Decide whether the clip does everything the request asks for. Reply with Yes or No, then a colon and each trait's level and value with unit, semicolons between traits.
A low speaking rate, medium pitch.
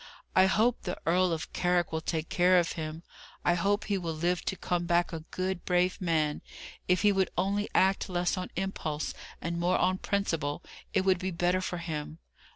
No: average, 195 wpm; medium, 180 Hz